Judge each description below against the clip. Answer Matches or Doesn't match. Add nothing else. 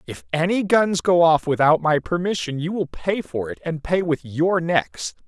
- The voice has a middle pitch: Matches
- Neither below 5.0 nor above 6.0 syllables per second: Doesn't match